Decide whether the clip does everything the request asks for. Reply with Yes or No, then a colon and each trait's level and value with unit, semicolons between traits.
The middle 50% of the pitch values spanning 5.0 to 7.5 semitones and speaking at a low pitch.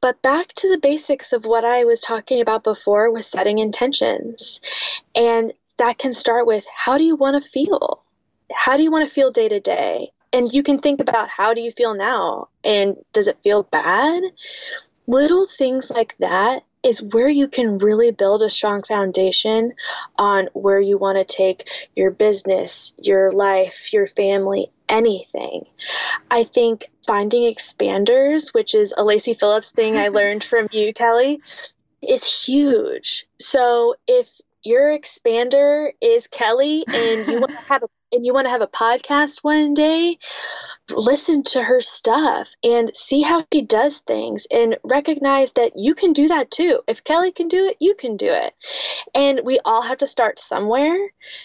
No: average, 5.3 semitones; very high, 255 Hz